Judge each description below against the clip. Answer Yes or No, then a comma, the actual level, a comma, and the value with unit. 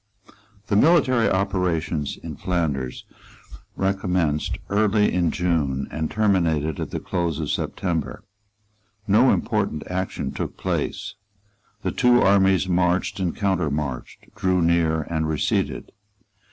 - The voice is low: Yes, very low, 90 Hz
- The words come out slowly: Yes, slow, 115 wpm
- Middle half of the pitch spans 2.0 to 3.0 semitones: No, average, 3.7 semitones